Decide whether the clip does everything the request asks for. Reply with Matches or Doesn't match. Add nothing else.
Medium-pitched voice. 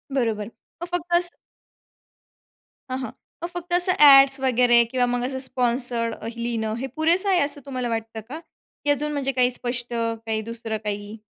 Doesn't match